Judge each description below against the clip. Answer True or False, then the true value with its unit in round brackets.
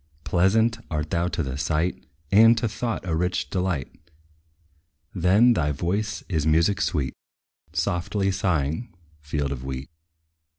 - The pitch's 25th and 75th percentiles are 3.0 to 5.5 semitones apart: True (4.7 semitones)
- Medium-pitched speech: False (85 Hz)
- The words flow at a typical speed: False (130 wpm)